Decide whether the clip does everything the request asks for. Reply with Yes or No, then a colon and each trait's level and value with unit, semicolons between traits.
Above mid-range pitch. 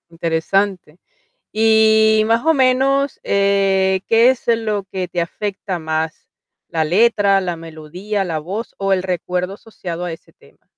Yes: high, 195 Hz